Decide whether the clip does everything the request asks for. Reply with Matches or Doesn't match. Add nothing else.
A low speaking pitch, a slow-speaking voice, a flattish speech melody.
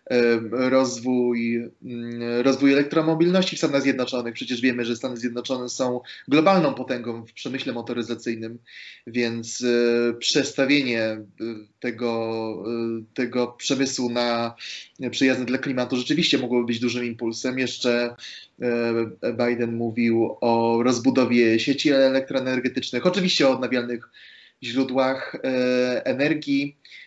Matches